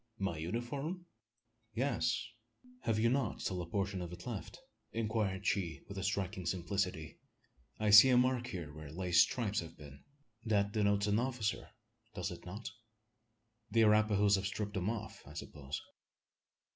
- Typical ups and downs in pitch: Yes, average, 3.9 semitones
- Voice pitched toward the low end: Yes, low, 100 Hz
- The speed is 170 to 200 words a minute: No, average, 155 wpm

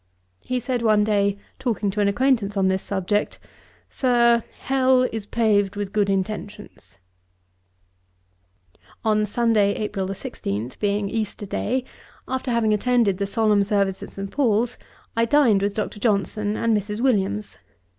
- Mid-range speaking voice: No, high, 210 Hz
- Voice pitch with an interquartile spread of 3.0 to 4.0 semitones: No, narrow, 2.6 semitones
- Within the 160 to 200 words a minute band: No, average, 140 wpm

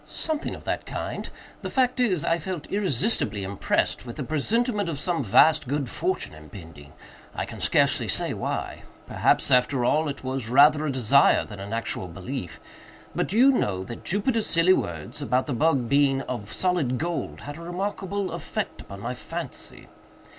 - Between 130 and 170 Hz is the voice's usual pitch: Yes, medium, 140 Hz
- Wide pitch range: Yes, wide, 7.4 semitones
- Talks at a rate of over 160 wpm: Yes, average, 170 wpm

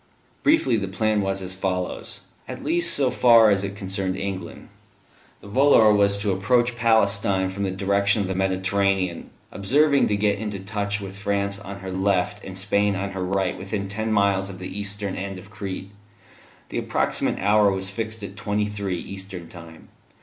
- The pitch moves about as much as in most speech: No, narrow, 1.6 semitones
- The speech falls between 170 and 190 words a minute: Yes, average, 180 wpm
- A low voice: Yes, low, 100 Hz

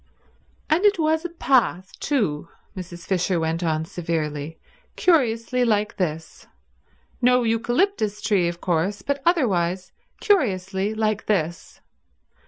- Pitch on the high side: Yes, high, 205 Hz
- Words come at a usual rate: No, slow, 115 wpm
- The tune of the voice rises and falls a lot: Yes, wide, 6.6 semitones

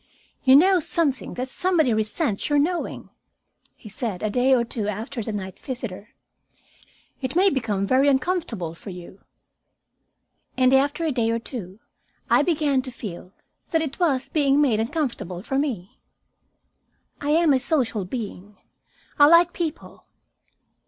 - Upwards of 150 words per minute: No, average, 145 wpm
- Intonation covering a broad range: Yes, wide, 5.8 semitones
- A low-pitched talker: No, very high, 260 Hz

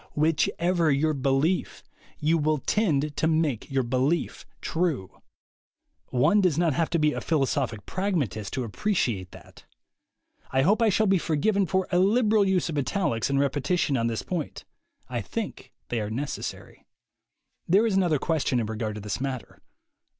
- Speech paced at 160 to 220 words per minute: Yes, average, 165 wpm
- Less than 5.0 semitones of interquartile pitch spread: No, wide, 5.6 semitones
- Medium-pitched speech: Yes, medium, 155 Hz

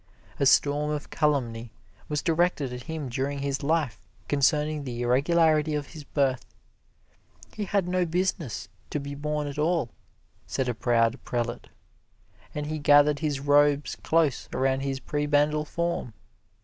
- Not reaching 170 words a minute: Yes, average, 145 wpm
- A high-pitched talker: No, medium, 145 Hz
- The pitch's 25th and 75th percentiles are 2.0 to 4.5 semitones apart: Yes, narrow, 2.5 semitones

